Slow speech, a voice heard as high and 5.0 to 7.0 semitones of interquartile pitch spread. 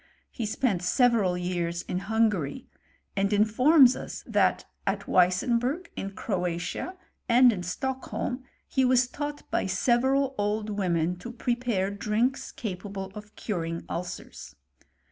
Yes: slow, 125 wpm; high, 210 Hz; wide, 5.5 semitones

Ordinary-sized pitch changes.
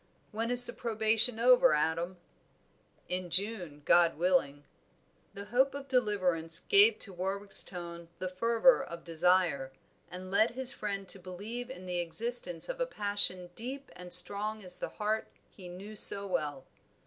Yes: average, 4.4 semitones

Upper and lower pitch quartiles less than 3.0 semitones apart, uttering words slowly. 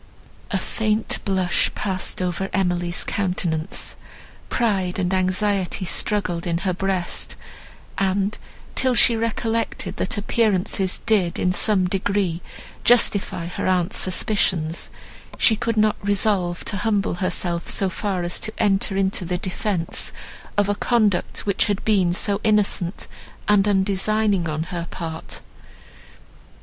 Yes: narrow, 2.6 semitones; slow, 125 wpm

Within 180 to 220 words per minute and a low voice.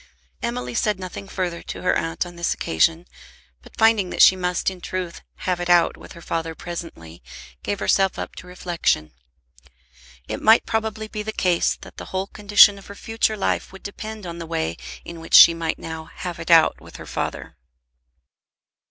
No: average, 185 wpm; medium, 180 Hz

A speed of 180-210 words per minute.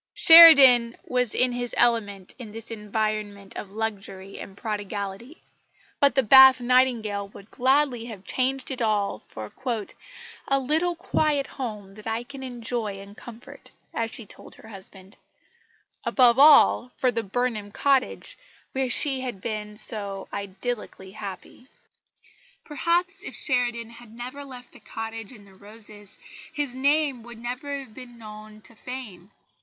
No: average, 145 wpm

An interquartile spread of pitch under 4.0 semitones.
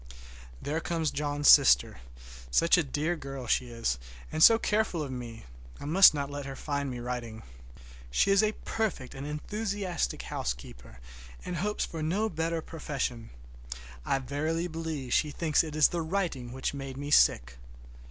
No: average, 4.5 semitones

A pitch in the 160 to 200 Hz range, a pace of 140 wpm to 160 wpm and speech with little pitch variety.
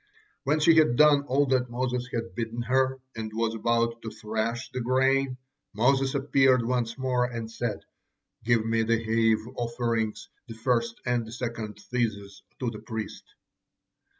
No: low, 120 Hz; average, 155 wpm; narrow, 2.2 semitones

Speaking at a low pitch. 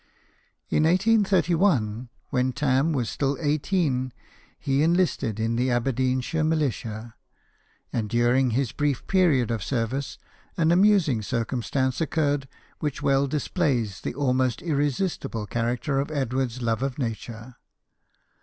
Yes: low, 130 Hz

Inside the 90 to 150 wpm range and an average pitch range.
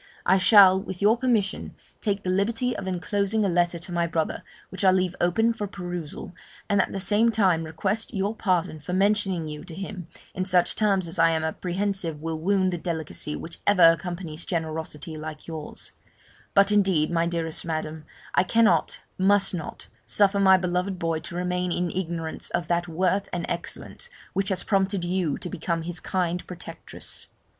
No: average, 180 wpm; average, 3.0 semitones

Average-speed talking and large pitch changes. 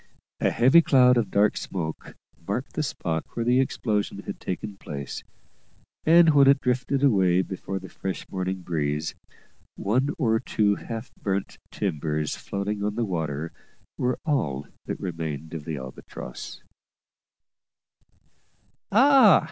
No: slow, 130 wpm; wide, 7.4 semitones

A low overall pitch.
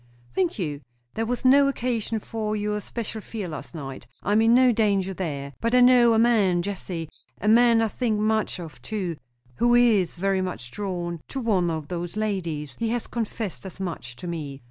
No: high, 205 Hz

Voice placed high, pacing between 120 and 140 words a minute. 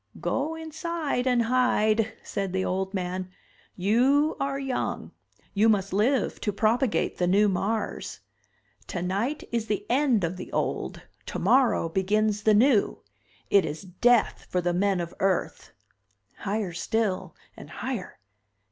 Yes: high, 210 Hz; slow, 135 wpm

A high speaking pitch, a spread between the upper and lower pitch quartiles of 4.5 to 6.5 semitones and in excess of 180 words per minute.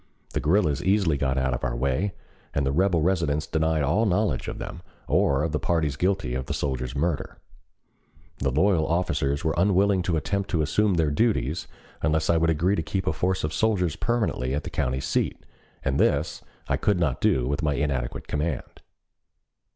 No: very low, 80 Hz; average, 4.9 semitones; average, 190 wpm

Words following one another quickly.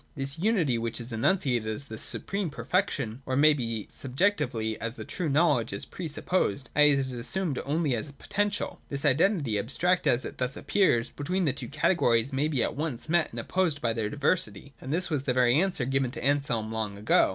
Yes: fast, 210 wpm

